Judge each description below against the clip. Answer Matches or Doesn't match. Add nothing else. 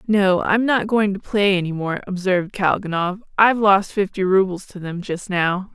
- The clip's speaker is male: Doesn't match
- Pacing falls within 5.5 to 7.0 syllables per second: Doesn't match